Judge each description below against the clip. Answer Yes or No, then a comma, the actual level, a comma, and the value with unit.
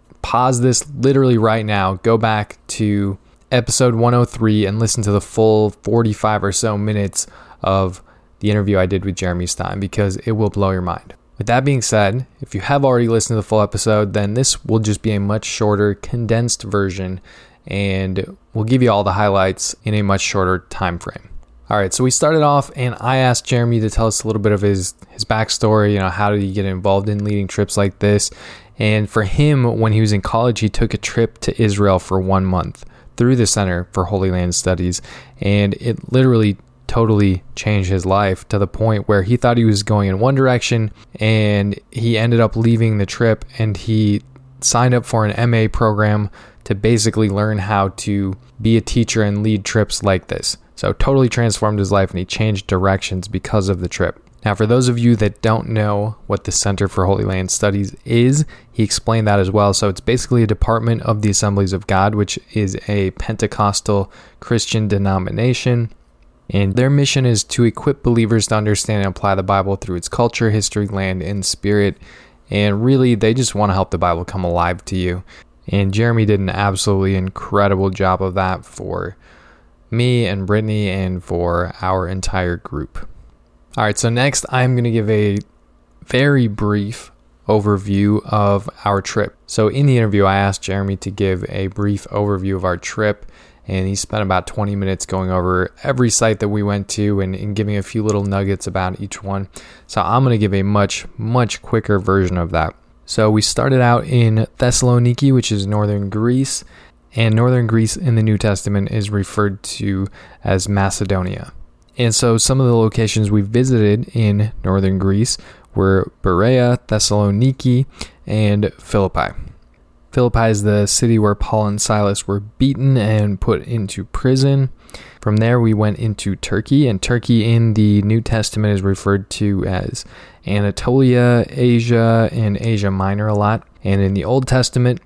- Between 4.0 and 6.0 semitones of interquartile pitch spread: No, average, 2.9 semitones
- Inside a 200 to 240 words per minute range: No, average, 185 wpm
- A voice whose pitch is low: Yes, low, 105 Hz